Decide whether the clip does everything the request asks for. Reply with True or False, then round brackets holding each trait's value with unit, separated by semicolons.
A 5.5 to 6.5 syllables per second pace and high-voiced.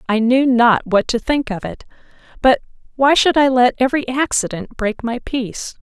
False (5.0 syllables/s; 245 Hz)